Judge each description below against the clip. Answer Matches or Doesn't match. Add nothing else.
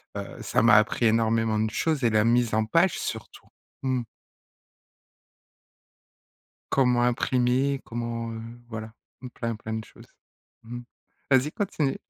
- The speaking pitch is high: Doesn't match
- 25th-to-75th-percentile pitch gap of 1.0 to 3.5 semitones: Matches